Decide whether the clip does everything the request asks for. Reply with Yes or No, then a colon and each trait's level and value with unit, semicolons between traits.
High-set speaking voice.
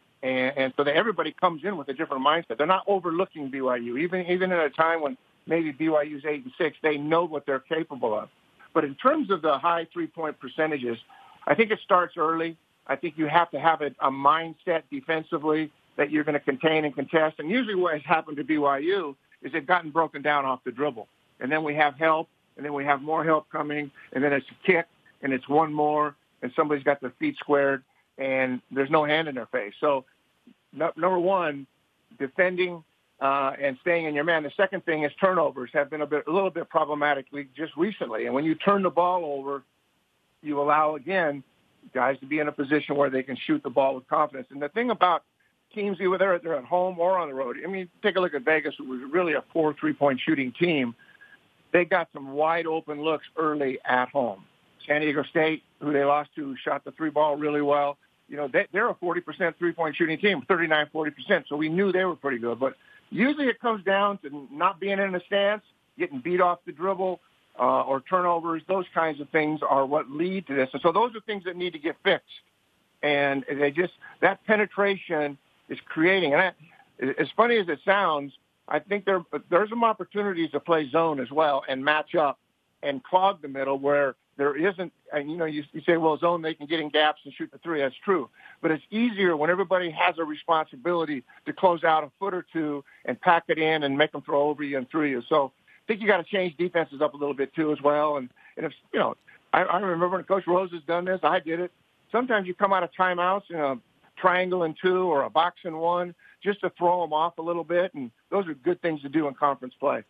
No: medium, 160 Hz